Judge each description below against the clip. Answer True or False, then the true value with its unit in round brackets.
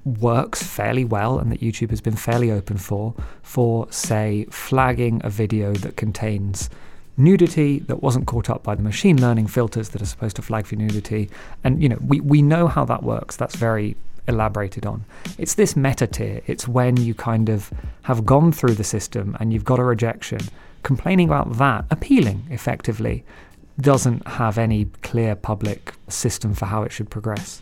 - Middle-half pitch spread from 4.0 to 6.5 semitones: False (3.4 semitones)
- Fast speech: False (180 wpm)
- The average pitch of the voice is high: False (115 Hz)